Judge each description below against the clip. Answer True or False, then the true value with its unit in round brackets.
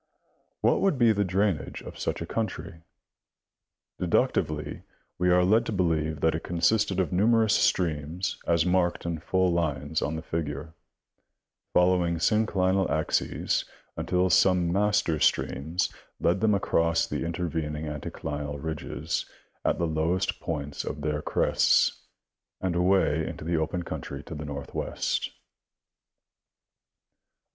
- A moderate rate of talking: False (130 wpm)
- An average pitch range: True (3.1 semitones)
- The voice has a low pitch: True (85 Hz)